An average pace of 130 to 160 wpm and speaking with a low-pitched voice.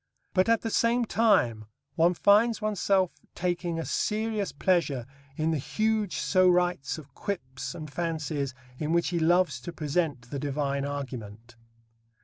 No: average, 140 wpm; medium, 165 Hz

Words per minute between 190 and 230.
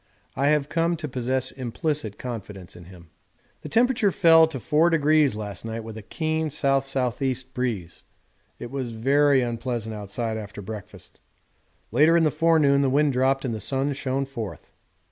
No: average, 160 wpm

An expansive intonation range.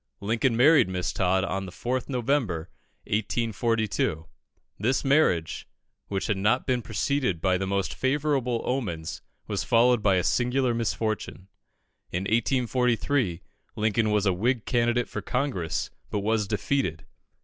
No: average, 4.5 semitones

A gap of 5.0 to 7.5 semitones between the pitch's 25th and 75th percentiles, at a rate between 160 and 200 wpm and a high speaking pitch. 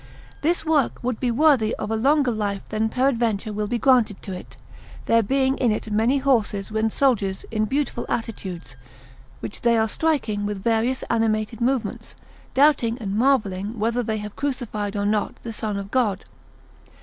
No: average, 3.6 semitones; average, 170 wpm; high, 225 Hz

